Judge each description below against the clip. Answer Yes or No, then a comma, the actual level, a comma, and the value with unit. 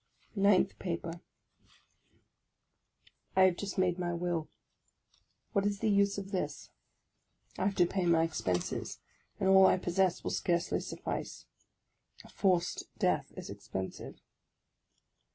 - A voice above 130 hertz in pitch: Yes, medium, 185 Hz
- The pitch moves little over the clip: Yes, narrow, 2.2 semitones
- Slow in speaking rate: Yes, slow, 125 wpm